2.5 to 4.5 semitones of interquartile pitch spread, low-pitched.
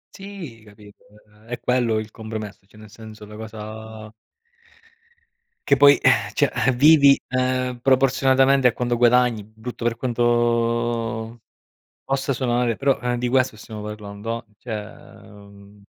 Yes: average, 2.8 semitones; low, 115 Hz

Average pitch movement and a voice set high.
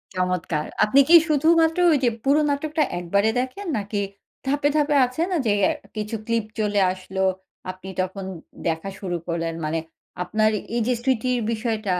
No: wide, 6.9 semitones; high, 215 Hz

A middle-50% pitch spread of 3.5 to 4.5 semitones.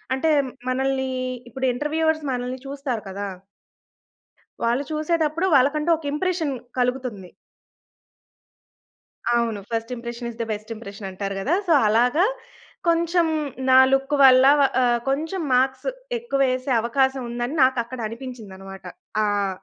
Yes: average, 4.1 semitones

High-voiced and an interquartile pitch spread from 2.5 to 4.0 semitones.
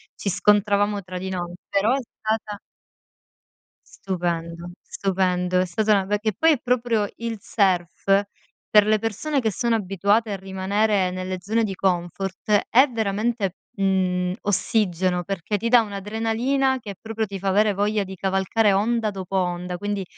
Yes: high, 200 Hz; average, 2.8 semitones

